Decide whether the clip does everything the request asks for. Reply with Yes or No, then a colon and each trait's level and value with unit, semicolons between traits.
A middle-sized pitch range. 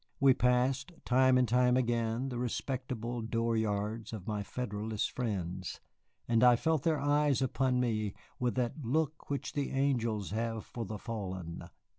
Yes: average, 3.0 semitones